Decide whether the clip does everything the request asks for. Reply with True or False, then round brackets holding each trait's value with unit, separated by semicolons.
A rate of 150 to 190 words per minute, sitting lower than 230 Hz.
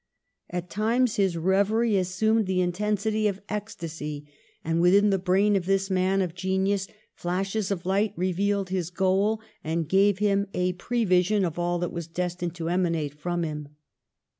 True (165 wpm; 185 Hz)